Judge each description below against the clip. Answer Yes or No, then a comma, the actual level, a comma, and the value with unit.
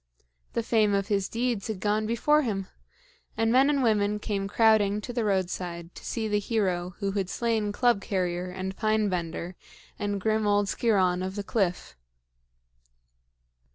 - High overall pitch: Yes, high, 205 Hz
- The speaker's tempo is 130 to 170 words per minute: Yes, average, 160 wpm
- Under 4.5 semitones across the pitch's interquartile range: Yes, average, 2.7 semitones